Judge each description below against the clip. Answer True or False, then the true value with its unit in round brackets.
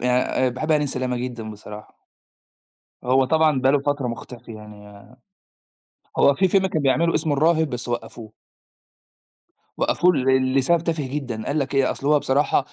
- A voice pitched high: False (130 Hz)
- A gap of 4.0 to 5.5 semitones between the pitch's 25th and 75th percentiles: False (3.6 semitones)